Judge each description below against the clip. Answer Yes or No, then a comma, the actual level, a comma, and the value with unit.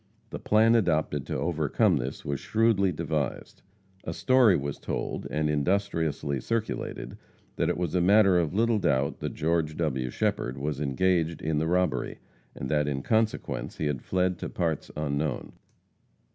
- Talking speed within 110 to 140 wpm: No, average, 160 wpm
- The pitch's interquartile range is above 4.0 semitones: Yes, average, 4.7 semitones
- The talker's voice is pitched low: Yes, very low, 80 Hz